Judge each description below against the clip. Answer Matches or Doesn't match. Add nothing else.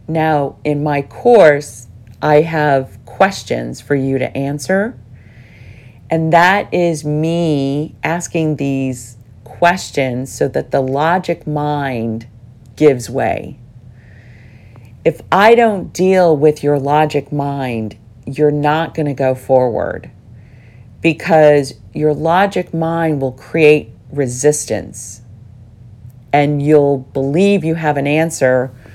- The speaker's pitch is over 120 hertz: Matches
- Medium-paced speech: Doesn't match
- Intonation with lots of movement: Doesn't match